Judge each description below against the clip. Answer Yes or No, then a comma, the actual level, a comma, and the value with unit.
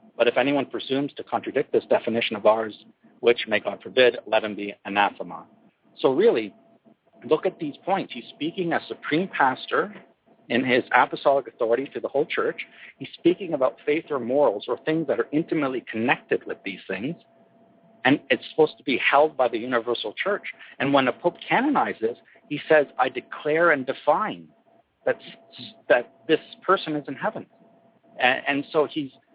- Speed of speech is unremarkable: Yes, average, 170 wpm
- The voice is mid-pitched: Yes, medium, 150 Hz